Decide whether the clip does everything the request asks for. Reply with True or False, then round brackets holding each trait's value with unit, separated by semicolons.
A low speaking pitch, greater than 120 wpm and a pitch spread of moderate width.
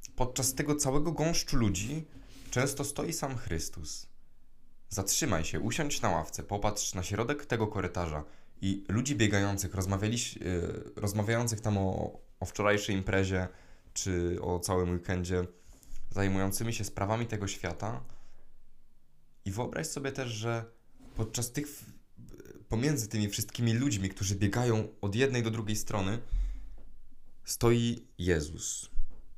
False (105 Hz; 115 wpm; 4.0 semitones)